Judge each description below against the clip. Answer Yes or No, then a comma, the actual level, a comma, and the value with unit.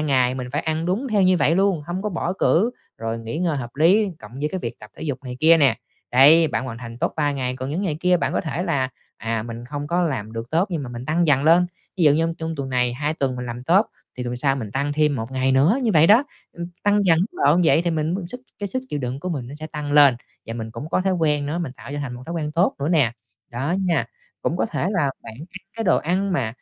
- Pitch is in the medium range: Yes, medium, 150 Hz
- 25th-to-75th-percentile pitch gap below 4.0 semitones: No, average, 5.2 semitones